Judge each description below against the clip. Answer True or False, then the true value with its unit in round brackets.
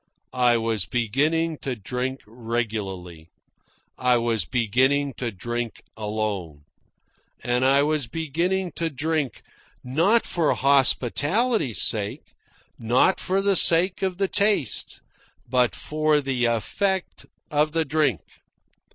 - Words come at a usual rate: False (115 wpm)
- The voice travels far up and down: True (5.9 semitones)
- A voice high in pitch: False (130 Hz)